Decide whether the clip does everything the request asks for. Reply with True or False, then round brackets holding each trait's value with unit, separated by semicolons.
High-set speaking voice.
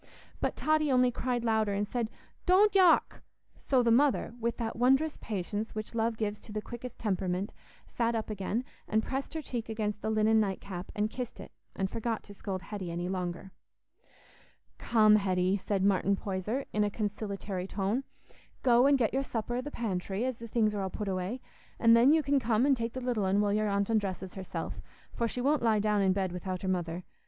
True (215 Hz)